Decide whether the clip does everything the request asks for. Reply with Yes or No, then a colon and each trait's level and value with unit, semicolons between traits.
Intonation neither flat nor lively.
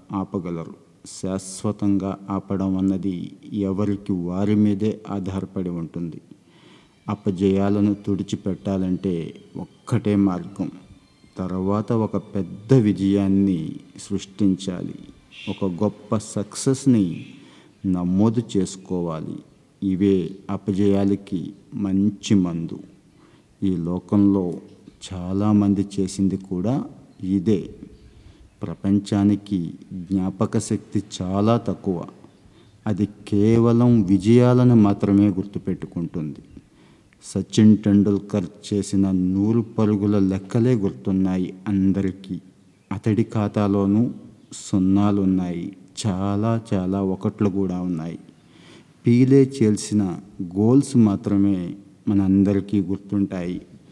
No: narrow, 1.5 semitones